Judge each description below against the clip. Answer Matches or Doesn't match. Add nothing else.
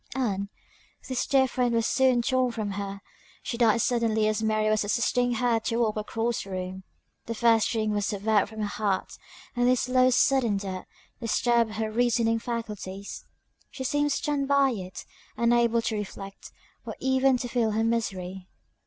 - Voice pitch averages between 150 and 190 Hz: Doesn't match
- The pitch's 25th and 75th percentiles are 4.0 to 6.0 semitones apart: Doesn't match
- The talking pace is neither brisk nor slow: Matches